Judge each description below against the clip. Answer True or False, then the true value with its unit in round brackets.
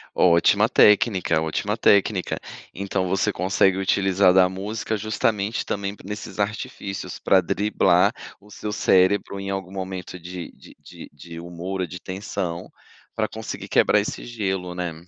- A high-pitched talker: False (95 Hz)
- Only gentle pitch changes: True (2.0 semitones)